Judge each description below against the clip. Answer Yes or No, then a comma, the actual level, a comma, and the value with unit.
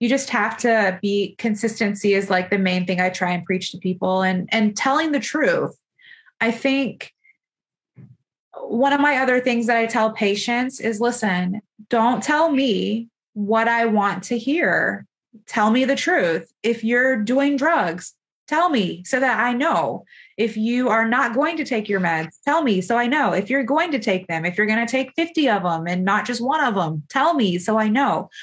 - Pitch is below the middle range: No, high, 230 Hz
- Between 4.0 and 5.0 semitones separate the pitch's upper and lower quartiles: Yes, average, 4.6 semitones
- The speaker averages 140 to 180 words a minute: No, fast, 205 wpm